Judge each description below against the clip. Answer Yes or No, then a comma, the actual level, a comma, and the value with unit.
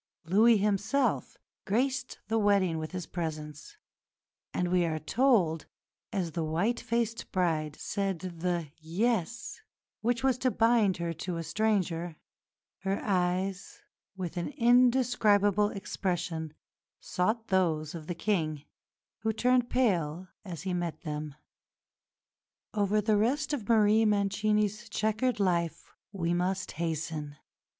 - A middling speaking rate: No, slow, 125 wpm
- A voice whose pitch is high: Yes, high, 195 Hz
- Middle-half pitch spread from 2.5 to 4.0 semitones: No, average, 4.6 semitones